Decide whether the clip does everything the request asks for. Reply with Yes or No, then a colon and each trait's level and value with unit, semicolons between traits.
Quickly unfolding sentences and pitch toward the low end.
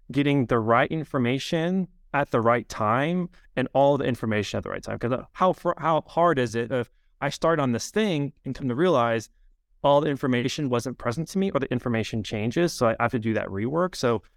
Yes: fast, 215 wpm; low, 130 Hz